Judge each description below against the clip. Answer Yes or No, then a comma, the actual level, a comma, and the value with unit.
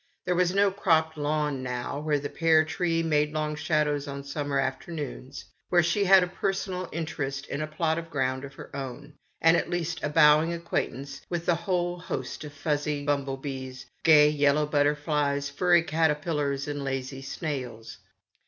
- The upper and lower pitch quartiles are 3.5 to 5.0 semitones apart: No, average, 2.8 semitones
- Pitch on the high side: No, medium, 150 Hz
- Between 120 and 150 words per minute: No, average, 170 wpm